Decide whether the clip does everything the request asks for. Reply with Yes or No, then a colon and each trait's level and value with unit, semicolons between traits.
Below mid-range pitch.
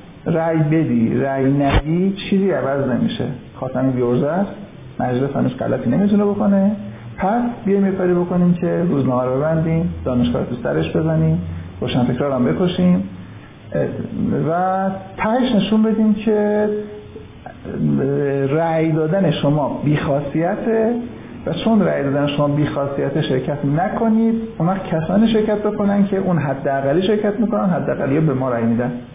No: medium, 160 Hz